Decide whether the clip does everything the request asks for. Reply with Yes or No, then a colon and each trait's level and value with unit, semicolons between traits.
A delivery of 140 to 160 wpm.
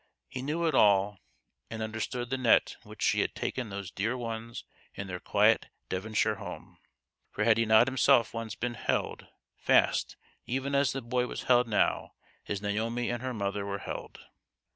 No: average, 180 wpm